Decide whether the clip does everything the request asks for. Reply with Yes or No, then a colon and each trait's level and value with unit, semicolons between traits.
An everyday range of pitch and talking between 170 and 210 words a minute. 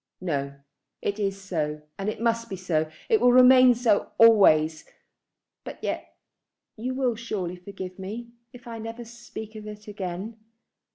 No: average, 4.2 semitones; average, 155 wpm